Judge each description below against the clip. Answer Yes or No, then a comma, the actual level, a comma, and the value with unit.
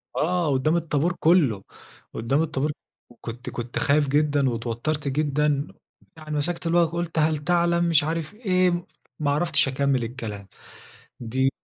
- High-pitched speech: No, medium, 150 Hz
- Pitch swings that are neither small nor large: Yes, average, 3.9 semitones